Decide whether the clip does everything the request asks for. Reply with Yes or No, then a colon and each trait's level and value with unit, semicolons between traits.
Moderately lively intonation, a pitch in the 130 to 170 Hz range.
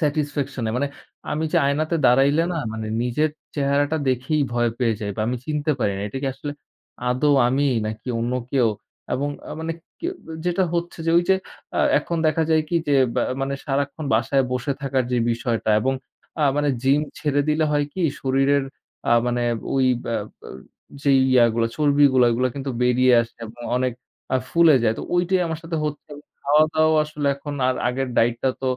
Yes: average, 3.4 semitones; medium, 140 Hz